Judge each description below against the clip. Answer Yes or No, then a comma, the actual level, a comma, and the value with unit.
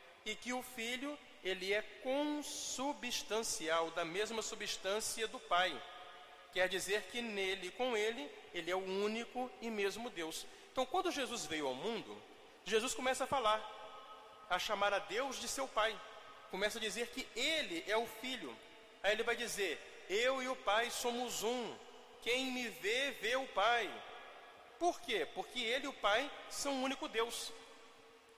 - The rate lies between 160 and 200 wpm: Yes, average, 165 wpm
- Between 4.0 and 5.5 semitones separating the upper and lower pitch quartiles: No, average, 3.6 semitones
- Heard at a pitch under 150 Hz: No, high, 230 Hz